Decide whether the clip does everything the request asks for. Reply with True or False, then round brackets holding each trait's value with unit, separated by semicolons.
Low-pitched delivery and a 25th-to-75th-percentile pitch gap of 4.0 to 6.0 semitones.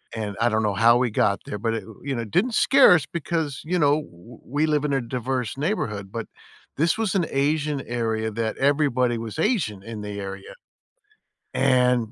True (125 Hz; 5.2 semitones)